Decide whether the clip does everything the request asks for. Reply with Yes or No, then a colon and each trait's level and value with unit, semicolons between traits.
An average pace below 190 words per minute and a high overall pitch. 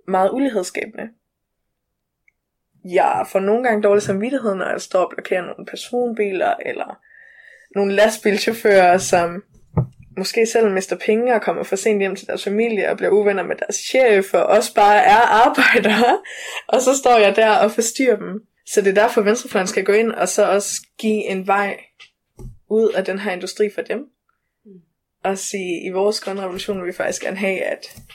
Yes: average, 180 wpm; high, 210 Hz